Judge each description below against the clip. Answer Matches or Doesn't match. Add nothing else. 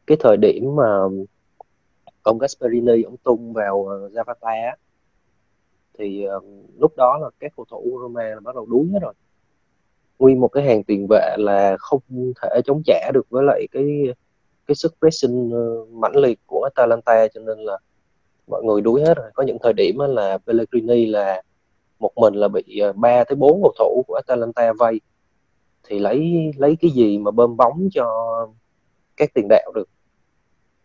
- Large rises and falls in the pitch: Doesn't match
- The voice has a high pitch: Doesn't match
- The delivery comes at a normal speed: Matches